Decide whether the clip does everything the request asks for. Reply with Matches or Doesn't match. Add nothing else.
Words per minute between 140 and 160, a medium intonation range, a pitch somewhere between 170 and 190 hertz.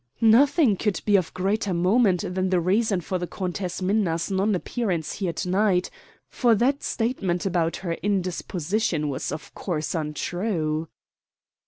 Matches